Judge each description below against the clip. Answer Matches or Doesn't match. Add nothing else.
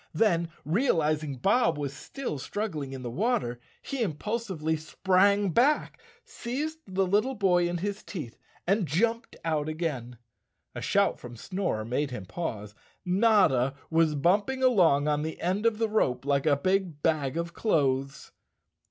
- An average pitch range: Doesn't match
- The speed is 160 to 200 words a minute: Doesn't match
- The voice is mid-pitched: Matches